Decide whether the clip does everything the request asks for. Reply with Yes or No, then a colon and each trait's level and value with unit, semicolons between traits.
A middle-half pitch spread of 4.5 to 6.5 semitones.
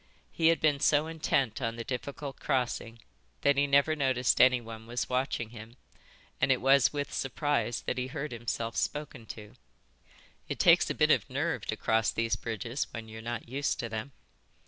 No: average, 3.6 semitones